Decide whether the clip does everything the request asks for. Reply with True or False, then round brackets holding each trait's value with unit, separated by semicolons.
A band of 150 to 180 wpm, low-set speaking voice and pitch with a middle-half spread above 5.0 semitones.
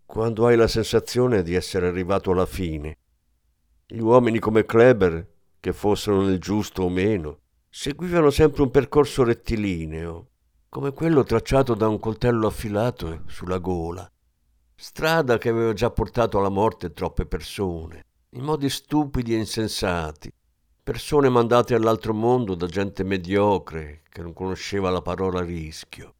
False (135 wpm; 100 Hz; 5.5 semitones)